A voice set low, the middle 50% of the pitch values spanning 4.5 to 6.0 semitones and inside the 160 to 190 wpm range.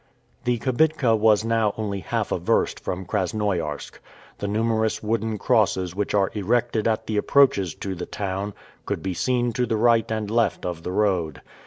No: low, 105 Hz; average, 3.1 semitones; average, 175 wpm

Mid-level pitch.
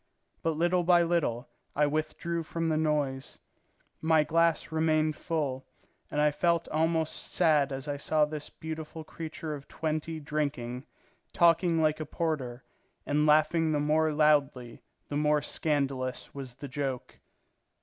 Yes: medium, 155 Hz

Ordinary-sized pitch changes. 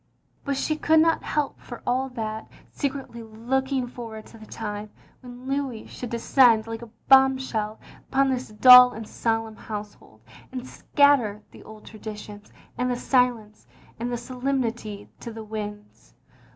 Yes: average, 3.3 semitones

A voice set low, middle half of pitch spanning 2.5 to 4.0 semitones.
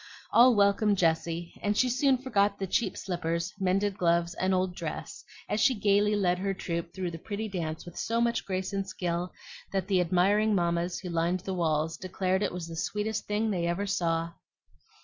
No: medium, 185 Hz; average, 3.1 semitones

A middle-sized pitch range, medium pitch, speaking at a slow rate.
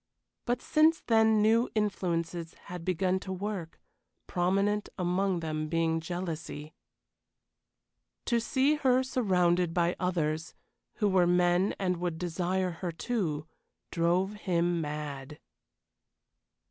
Yes: average, 3.6 semitones; medium, 180 Hz; slow, 110 wpm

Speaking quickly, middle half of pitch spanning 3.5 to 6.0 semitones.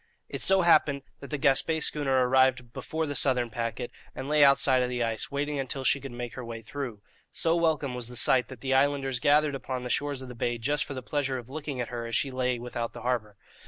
No: fast, 240 wpm; average, 2.7 semitones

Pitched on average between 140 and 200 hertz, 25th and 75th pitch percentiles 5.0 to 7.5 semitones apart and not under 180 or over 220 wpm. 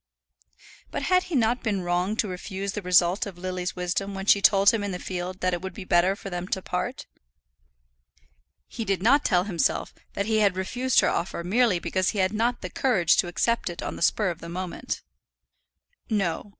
No: high, 190 Hz; average, 3.0 semitones; fast, 205 wpm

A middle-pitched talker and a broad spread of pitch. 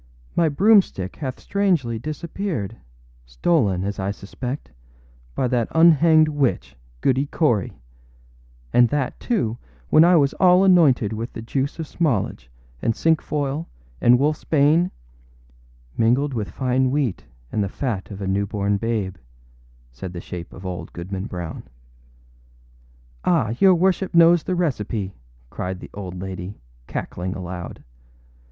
No: low, 125 Hz; wide, 8.1 semitones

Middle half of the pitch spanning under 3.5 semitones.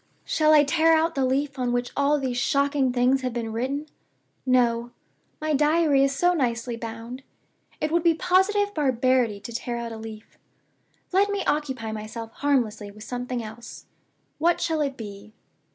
No: average, 4.5 semitones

